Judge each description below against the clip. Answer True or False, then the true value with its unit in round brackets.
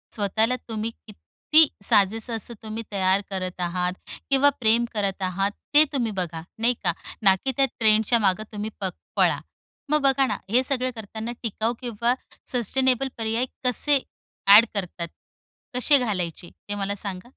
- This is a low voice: False (220 Hz)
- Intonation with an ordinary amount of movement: True (4.1 semitones)